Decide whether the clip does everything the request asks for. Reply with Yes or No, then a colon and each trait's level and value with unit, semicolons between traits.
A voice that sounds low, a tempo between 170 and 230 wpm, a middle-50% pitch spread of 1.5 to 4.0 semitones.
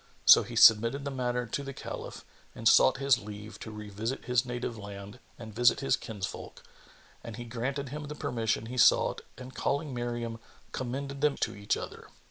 Yes: low, 120 Hz; average, 180 wpm; average, 3.2 semitones